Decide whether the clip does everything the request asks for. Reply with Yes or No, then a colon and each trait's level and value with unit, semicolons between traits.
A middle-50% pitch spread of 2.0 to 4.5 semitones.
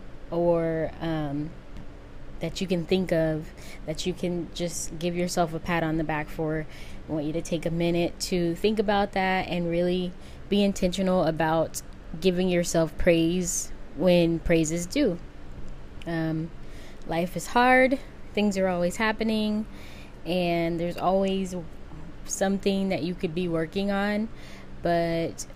Yes: narrow, 2.6 semitones